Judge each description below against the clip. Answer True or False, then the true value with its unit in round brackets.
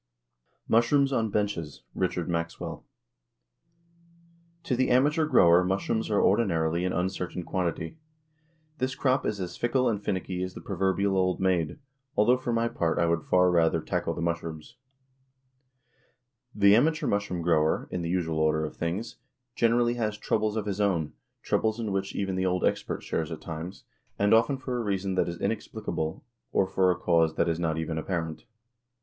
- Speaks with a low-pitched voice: True (95 Hz)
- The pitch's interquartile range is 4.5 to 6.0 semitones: True (4.8 semitones)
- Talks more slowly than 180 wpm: True (165 wpm)